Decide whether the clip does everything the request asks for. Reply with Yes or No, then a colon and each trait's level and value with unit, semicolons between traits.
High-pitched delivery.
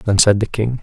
No: low, 110 Hz